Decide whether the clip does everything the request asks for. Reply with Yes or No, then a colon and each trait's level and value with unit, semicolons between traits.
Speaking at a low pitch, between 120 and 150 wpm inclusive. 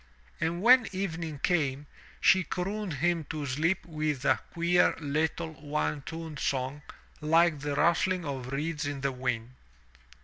No: medium, 155 Hz; average, 140 wpm